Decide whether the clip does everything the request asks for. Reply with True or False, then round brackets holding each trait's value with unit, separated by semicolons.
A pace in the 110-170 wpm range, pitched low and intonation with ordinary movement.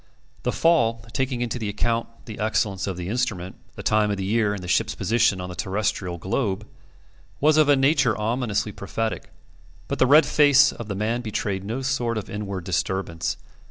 False (185 wpm; 110 Hz; 4.1 semitones)